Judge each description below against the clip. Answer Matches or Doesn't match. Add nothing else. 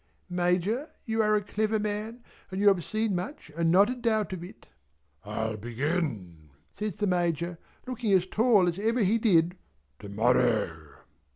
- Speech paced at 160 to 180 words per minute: Matches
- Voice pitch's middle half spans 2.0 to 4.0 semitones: Doesn't match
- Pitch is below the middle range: Doesn't match